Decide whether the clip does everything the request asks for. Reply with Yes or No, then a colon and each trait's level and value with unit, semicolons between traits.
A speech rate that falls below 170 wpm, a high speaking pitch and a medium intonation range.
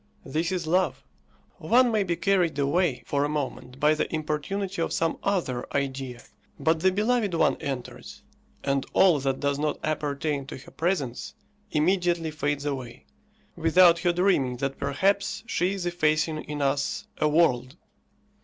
No: average, 155 wpm; medium, 155 Hz; average, 4.2 semitones